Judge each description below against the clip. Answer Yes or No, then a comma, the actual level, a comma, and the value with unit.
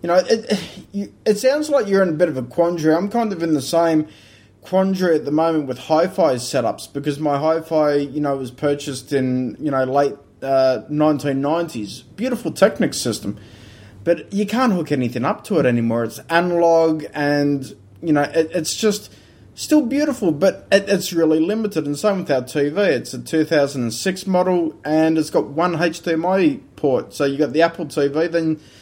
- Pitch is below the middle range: No, medium, 160 Hz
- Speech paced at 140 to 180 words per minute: No, average, 190 wpm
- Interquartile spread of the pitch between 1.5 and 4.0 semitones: No, average, 4.4 semitones